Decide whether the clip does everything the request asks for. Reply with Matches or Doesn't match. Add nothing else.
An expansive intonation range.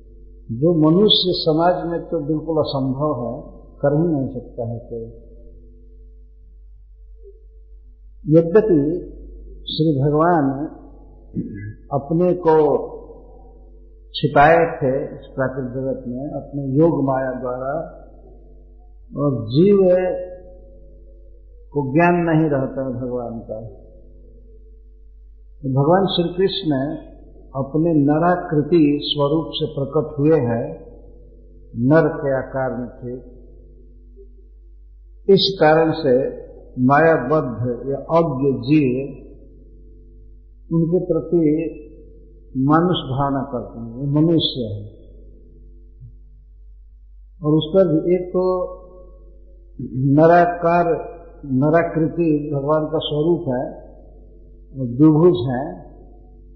Matches